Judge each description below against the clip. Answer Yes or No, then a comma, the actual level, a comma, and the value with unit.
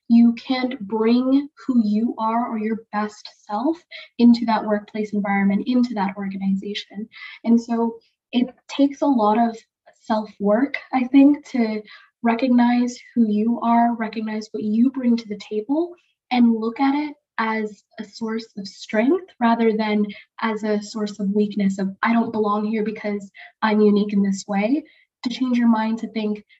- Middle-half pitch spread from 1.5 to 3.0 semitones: Yes, average, 2.7 semitones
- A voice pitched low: No, high, 225 Hz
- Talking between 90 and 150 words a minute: No, average, 165 wpm